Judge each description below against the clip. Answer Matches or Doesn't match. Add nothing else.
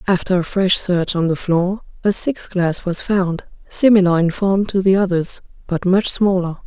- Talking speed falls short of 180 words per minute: Doesn't match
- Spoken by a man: Doesn't match